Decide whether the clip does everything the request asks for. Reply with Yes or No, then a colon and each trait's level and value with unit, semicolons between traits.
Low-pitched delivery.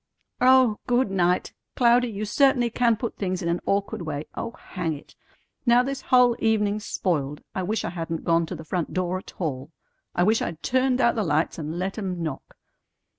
No: high, 195 Hz